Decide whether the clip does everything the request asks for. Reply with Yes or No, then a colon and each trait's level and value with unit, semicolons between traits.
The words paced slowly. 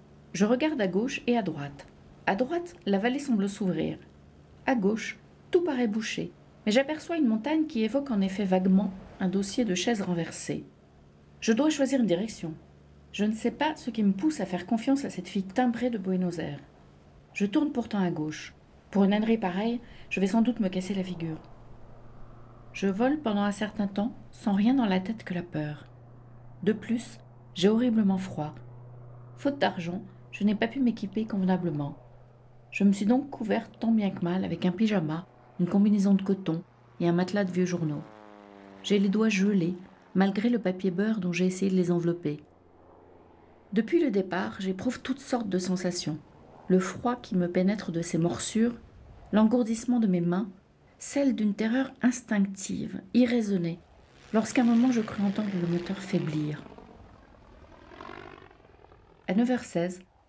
No: average, 170 wpm